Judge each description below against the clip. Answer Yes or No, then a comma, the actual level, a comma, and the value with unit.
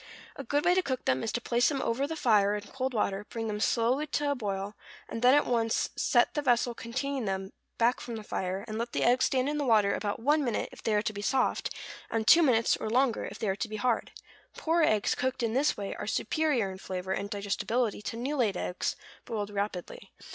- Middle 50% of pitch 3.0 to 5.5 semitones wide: Yes, average, 4.1 semitones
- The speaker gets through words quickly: Yes, fast, 240 wpm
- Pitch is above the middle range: Yes, high, 230 Hz